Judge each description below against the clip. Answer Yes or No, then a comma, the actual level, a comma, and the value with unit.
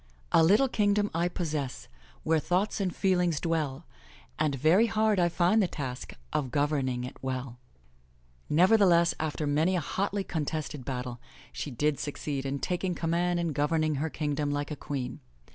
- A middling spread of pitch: Yes, average, 3.8 semitones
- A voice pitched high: No, medium, 155 Hz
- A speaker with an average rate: Yes, average, 160 wpm